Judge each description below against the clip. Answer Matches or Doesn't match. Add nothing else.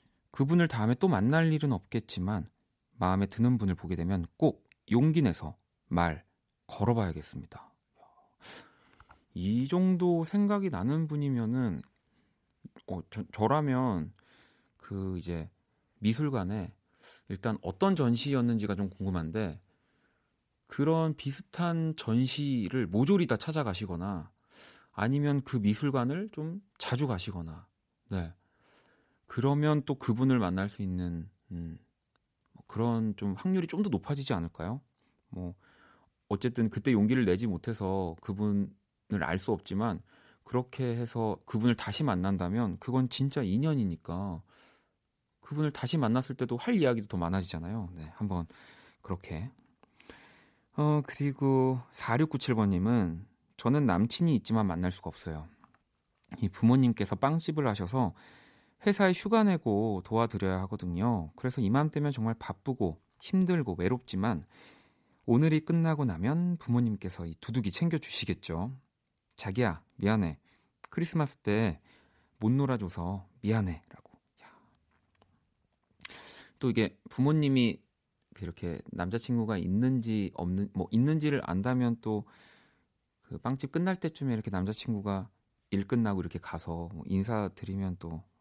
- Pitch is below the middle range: Matches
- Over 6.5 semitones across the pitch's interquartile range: Doesn't match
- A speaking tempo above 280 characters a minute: Doesn't match